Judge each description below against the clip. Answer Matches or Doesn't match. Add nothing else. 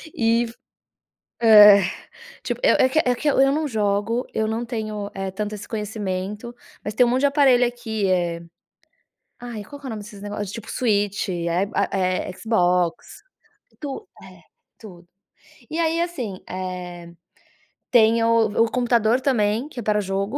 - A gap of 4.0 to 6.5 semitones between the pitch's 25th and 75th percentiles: Doesn't match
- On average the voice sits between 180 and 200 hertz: Doesn't match